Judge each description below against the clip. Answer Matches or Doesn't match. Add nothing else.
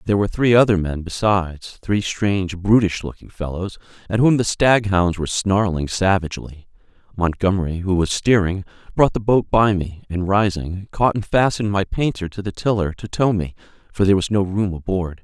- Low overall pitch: Matches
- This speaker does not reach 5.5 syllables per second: Matches